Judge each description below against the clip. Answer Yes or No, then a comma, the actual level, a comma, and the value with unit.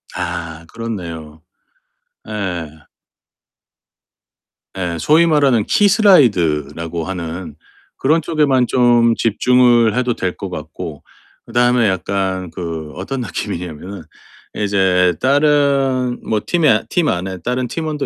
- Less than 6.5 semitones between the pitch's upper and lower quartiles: No, wide, 6.8 semitones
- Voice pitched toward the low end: Yes, low, 105 Hz